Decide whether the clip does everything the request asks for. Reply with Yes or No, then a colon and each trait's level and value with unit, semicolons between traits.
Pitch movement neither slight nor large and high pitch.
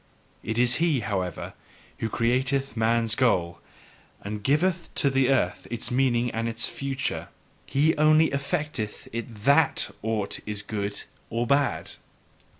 No: average, 3.8 semitones; low, 120 Hz